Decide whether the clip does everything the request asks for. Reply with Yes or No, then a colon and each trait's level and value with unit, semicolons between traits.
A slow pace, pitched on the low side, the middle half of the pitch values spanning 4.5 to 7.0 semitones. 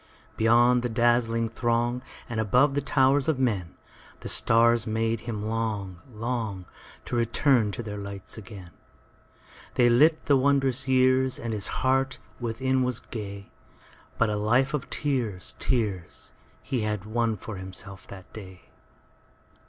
No: slow, 120 wpm; low, 115 Hz; average, 3.4 semitones